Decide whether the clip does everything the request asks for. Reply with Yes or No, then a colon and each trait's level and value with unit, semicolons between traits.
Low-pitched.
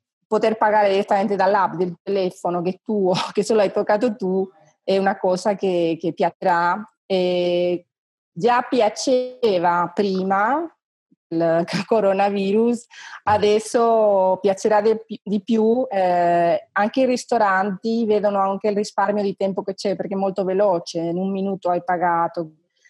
No: high, 195 Hz